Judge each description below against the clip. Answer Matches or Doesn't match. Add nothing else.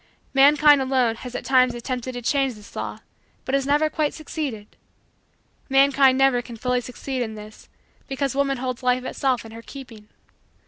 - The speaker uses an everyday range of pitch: Doesn't match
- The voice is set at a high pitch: Matches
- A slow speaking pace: Doesn't match